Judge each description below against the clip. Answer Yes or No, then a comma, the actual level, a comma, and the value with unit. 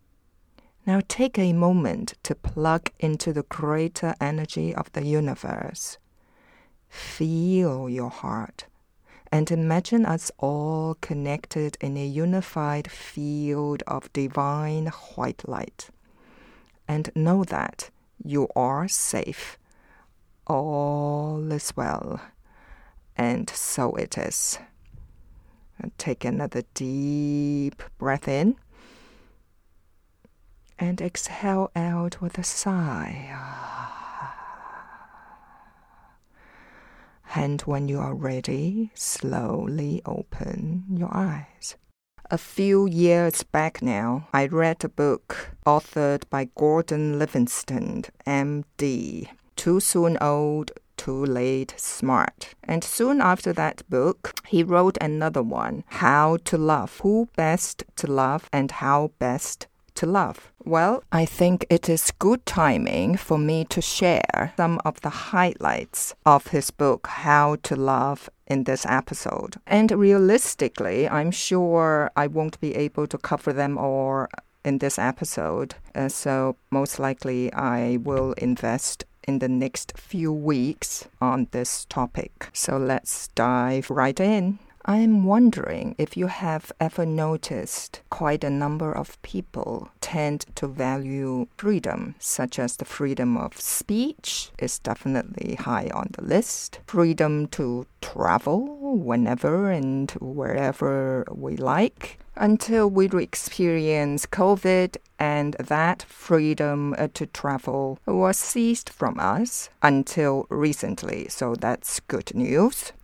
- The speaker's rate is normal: No, slow, 115 wpm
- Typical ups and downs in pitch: Yes, average, 4.4 semitones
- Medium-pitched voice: Yes, medium, 155 Hz